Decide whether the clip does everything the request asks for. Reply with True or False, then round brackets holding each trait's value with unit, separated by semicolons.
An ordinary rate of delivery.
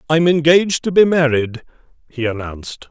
True (145 wpm)